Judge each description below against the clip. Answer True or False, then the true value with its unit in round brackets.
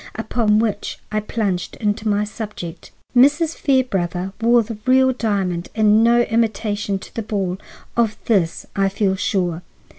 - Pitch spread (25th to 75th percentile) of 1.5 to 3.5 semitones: True (3.0 semitones)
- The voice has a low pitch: False (210 Hz)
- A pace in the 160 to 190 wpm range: False (145 wpm)